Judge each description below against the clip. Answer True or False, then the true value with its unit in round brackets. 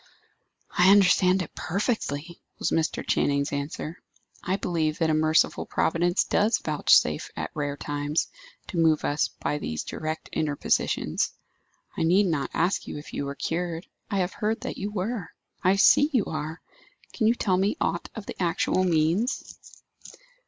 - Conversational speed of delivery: True (160 wpm)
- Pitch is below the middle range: False (165 Hz)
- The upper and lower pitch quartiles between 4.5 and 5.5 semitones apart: False (4.0 semitones)